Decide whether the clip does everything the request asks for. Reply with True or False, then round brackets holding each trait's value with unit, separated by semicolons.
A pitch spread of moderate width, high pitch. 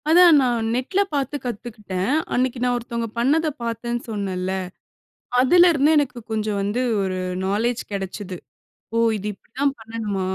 True (4.2 semitones; 235 Hz)